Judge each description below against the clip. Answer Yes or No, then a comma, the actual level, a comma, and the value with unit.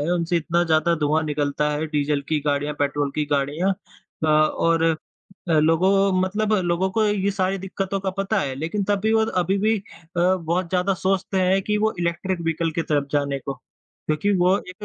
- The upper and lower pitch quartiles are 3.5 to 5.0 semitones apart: Yes, average, 4.0 semitones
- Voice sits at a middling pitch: Yes, medium, 170 Hz